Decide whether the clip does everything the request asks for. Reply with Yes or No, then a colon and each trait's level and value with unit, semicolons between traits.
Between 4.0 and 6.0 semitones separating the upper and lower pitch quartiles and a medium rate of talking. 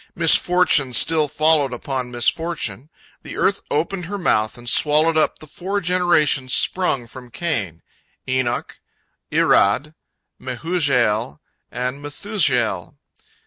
No: average, 5.2 semitones; slow, 105 wpm